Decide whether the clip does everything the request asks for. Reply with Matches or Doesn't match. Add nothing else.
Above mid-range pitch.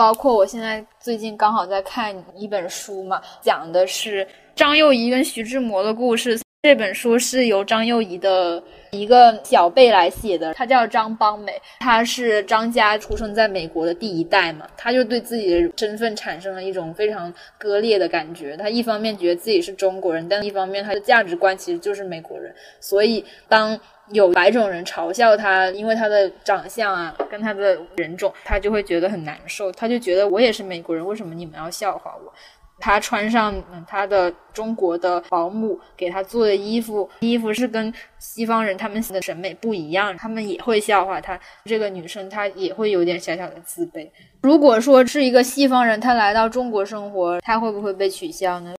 Matches